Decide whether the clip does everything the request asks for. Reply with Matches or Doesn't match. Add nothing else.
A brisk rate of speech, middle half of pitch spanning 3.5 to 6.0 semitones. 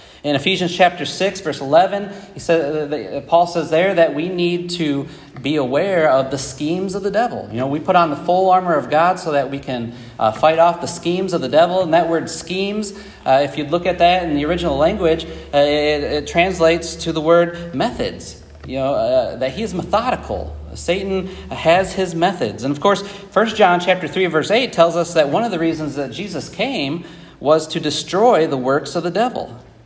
Matches